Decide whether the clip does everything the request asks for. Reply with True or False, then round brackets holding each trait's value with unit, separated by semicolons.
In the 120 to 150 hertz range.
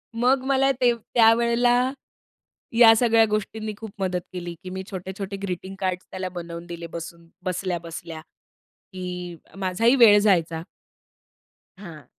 False (190 Hz)